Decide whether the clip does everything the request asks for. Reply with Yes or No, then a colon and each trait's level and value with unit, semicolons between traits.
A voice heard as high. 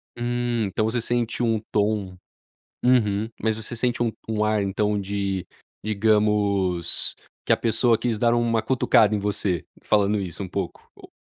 No: low, 105 Hz